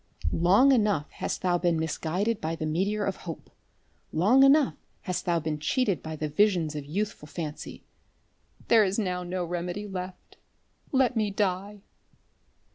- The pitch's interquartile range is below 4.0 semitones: No, average, 4.3 semitones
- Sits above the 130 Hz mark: Yes, medium, 185 Hz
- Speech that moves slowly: No, average, 150 wpm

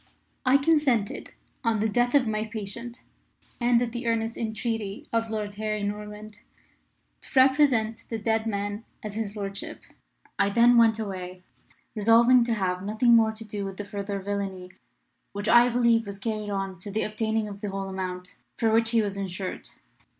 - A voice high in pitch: Yes, high, 215 Hz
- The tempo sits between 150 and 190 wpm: Yes, average, 170 wpm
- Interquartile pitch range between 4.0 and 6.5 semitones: No, narrow, 2.4 semitones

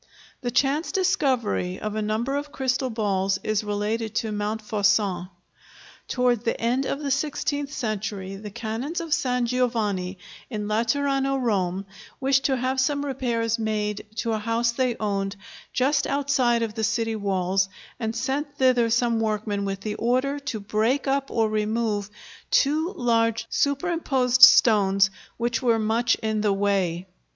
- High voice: Yes, high, 230 Hz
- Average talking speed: Yes, average, 150 wpm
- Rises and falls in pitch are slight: No, average, 4.0 semitones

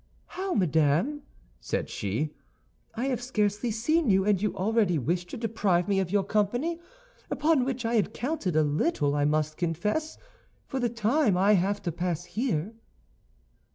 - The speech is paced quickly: No, average, 160 wpm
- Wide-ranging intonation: Yes, wide, 5.8 semitones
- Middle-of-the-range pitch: No, high, 205 Hz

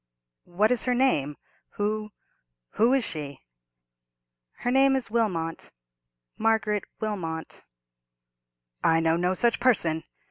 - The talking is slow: Yes, slow, 95 wpm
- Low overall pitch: No, high, 190 Hz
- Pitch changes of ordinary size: No, wide, 6.4 semitones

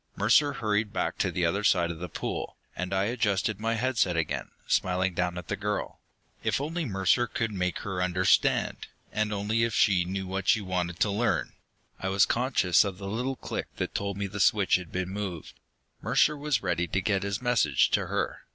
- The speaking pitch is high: No, low, 100 Hz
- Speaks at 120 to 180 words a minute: No, fast, 205 wpm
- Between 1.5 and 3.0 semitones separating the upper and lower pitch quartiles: No, average, 3.4 semitones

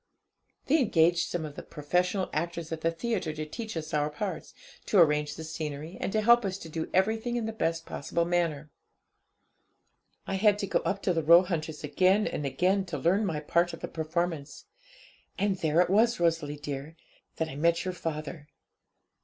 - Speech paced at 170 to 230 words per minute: Yes, average, 185 wpm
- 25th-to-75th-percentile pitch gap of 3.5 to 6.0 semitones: Yes, average, 3.8 semitones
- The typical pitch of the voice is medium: Yes, medium, 170 Hz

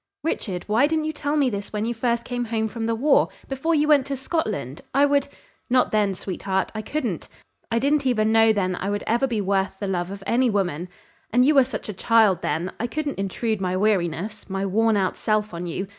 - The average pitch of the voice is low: No, high, 220 Hz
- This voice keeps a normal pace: No, fast, 230 wpm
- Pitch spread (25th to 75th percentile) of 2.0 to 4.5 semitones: No, average, 4.9 semitones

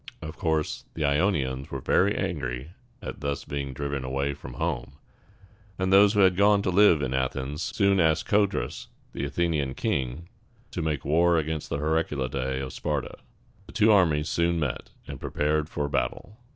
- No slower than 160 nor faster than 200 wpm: Yes, average, 165 wpm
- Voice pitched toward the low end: Yes, very low, 75 Hz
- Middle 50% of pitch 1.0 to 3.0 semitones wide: No, average, 4.1 semitones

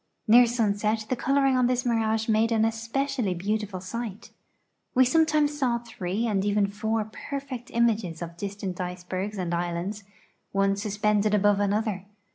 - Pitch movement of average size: Yes, average, 3.1 semitones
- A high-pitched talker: Yes, high, 215 Hz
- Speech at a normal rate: Yes, average, 145 wpm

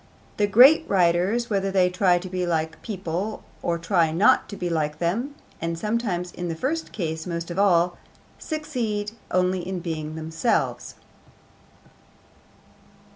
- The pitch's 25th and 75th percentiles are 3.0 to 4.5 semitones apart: Yes, average, 3.6 semitones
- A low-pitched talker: No, medium, 180 Hz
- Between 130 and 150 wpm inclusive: Yes, average, 145 wpm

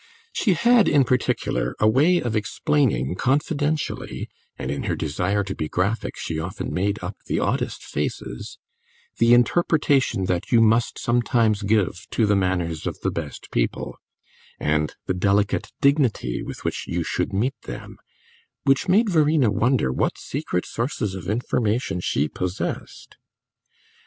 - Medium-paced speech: Yes, average, 145 wpm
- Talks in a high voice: No, low, 110 Hz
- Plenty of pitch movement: Yes, wide, 6.7 semitones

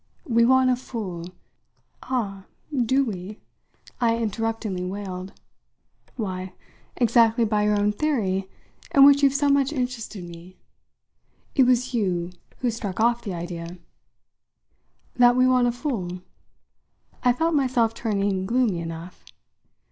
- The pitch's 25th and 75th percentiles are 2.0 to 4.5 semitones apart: No, average, 5.0 semitones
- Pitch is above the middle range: Yes, high, 225 Hz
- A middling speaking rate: No, slow, 130 wpm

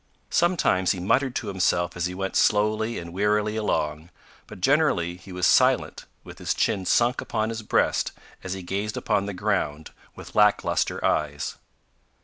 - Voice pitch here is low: Yes, low, 100 Hz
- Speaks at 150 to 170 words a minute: Yes, average, 165 wpm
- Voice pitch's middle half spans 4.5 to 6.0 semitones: No, average, 3.4 semitones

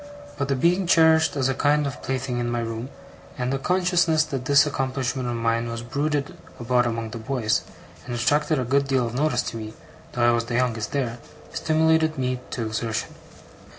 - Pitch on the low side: Yes, low, 130 Hz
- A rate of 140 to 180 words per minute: No, average, 195 wpm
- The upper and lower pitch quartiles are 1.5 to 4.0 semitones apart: Yes, average, 3.7 semitones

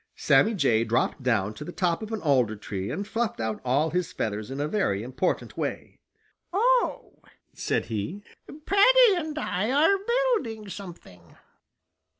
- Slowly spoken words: No, average, 155 wpm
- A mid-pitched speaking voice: Yes, medium, 180 Hz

